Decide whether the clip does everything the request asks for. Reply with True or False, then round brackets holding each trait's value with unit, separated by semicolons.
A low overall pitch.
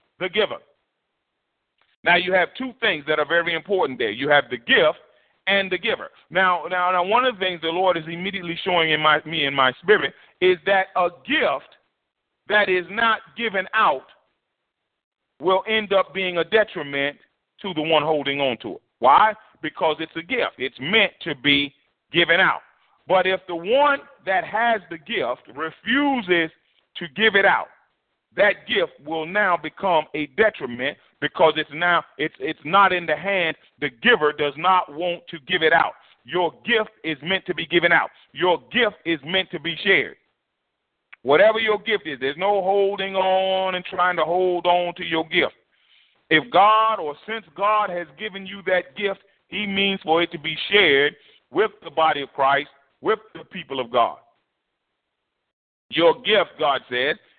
False (180 Hz)